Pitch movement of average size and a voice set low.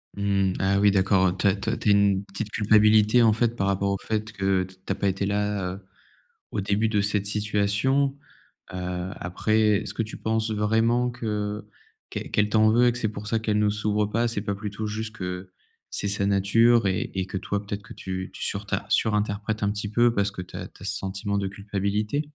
No: narrow, 1.7 semitones; low, 105 Hz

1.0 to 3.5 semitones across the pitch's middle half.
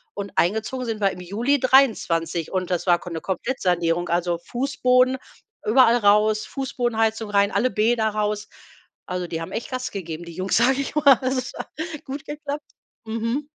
No: wide, 5.7 semitones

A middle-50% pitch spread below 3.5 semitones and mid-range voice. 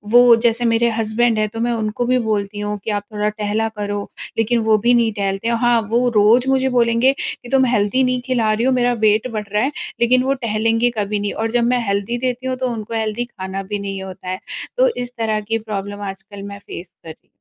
No: average, 2.8 semitones; high, 225 Hz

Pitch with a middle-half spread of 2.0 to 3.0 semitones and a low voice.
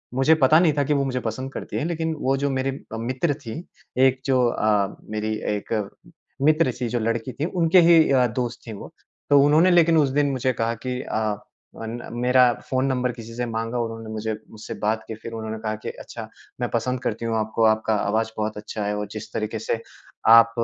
No: average, 3.4 semitones; low, 120 Hz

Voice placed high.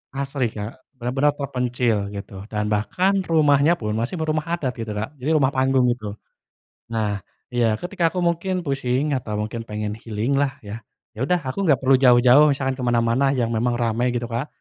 No: low, 125 Hz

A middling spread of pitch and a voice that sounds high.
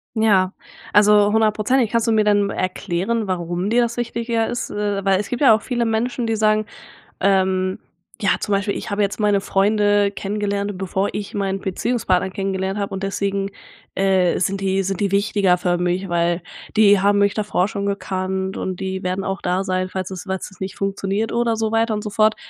No: narrow, 2.1 semitones; high, 200 Hz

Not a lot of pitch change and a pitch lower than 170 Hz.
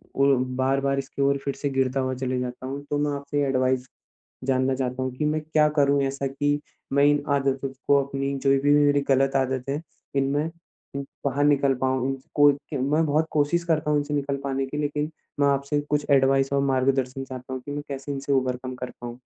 Yes: narrow, 1.5 semitones; medium, 140 Hz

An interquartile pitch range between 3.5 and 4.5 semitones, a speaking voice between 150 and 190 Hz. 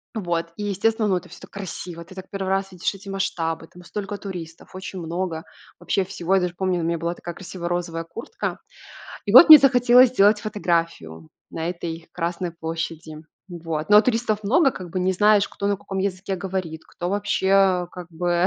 No: average, 3.0 semitones; medium, 185 Hz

